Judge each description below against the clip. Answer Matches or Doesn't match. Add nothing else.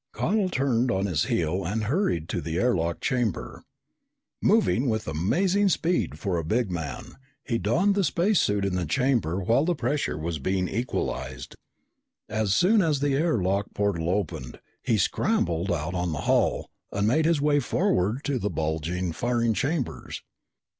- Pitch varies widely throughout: Matches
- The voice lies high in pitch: Doesn't match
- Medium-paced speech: Matches